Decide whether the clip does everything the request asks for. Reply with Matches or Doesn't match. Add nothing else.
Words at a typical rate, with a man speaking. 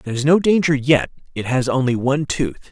Doesn't match